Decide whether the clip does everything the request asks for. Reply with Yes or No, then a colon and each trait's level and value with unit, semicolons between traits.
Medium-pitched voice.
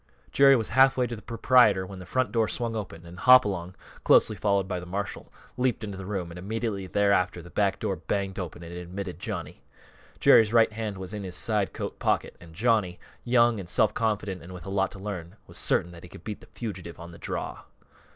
No: low, 100 Hz